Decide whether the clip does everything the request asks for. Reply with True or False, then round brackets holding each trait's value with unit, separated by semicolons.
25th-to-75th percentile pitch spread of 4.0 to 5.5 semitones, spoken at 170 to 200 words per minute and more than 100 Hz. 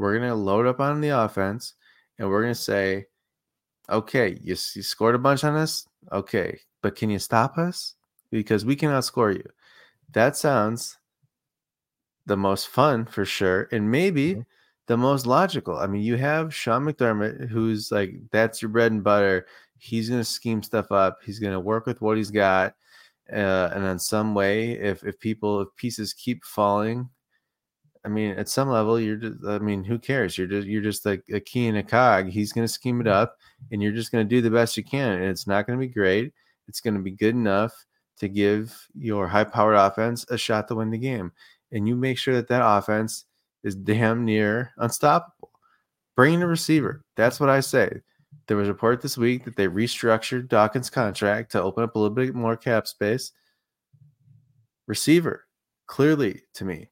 False (3.2 semitones; 195 wpm; 110 Hz)